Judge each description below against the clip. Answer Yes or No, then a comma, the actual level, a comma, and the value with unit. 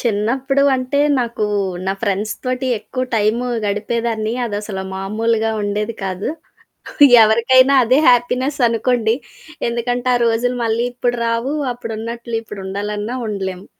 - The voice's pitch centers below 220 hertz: No, high, 230 Hz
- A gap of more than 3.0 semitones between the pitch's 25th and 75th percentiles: No, average, 2.7 semitones